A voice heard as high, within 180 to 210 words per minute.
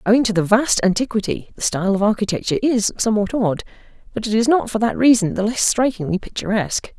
Yes: high, 215 Hz; average, 200 wpm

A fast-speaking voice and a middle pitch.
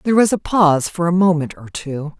Yes: fast, 245 wpm; medium, 170 Hz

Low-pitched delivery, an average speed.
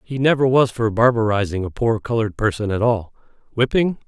Yes: low, 115 Hz; average, 175 wpm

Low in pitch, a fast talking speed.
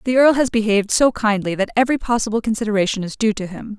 No: high, 220 Hz; fast, 220 wpm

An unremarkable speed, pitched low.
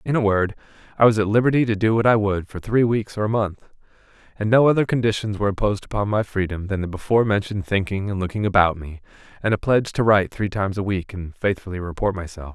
No: fast, 235 wpm; low, 105 Hz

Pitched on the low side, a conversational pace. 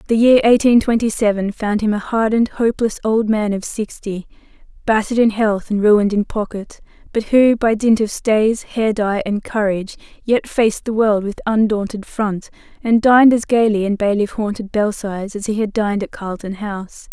No: high, 215 Hz; average, 185 wpm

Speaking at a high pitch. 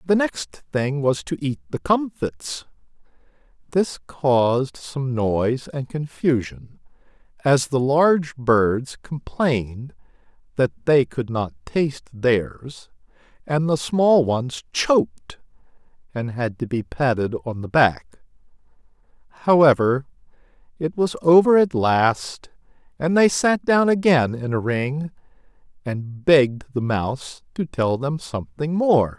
No: low, 135 Hz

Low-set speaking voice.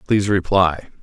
Yes: very low, 95 Hz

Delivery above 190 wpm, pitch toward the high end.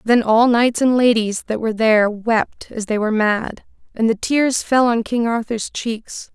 Yes: average, 200 wpm; high, 225 Hz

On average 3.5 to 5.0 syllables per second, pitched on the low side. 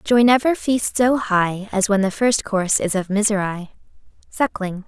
No: 4.6 syllables/s; high, 210 Hz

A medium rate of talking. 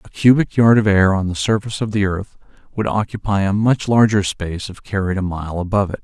No: fast, 230 wpm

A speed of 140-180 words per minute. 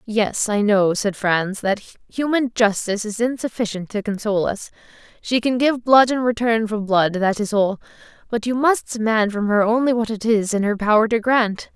No: average, 200 wpm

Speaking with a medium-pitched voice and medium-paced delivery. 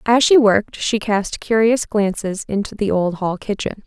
No: high, 210 Hz; average, 185 wpm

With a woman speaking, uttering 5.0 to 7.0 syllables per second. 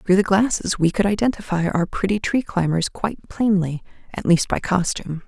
Yes: female; 5.5 syllables/s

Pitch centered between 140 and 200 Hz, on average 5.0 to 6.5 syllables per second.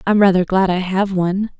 Yes: high, 190 Hz; 5.6 syllables/s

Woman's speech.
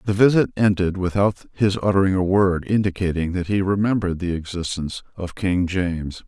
No: male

